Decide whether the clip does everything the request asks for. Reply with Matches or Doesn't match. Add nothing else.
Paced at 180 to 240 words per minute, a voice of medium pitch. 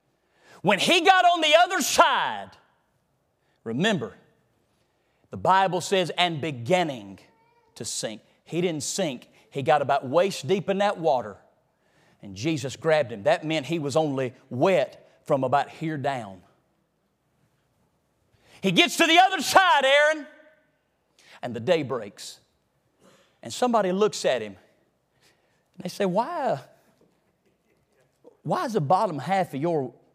Doesn't match